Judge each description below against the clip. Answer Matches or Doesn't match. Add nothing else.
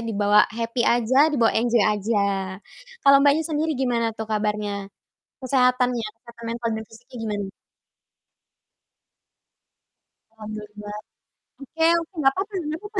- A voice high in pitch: Matches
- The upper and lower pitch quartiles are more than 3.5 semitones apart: Matches